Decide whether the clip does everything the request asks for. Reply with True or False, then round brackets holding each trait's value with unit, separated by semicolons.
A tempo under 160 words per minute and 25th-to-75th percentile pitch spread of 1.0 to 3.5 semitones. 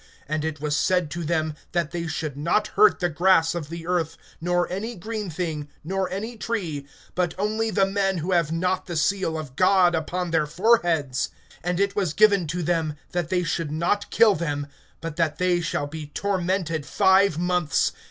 False (190 wpm; 3.2 semitones)